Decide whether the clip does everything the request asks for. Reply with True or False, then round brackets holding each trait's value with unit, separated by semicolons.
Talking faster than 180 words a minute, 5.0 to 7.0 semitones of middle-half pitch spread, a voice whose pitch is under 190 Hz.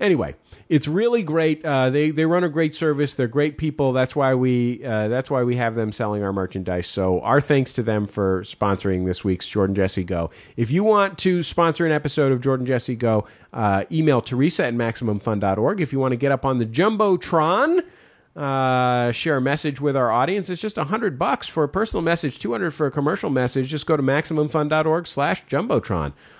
True (200 wpm; 5.3 semitones; 140 Hz)